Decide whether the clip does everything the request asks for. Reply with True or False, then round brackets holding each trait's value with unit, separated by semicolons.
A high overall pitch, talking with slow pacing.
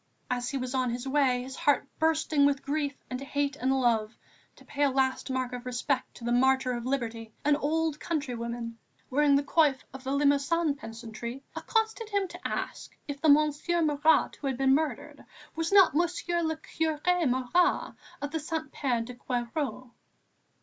False (280 Hz; 175 wpm)